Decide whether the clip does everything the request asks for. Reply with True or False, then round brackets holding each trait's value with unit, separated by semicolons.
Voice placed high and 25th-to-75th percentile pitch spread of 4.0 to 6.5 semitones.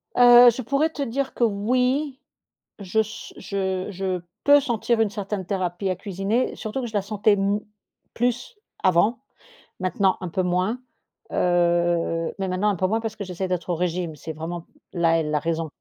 True (195 Hz; 4.3 semitones)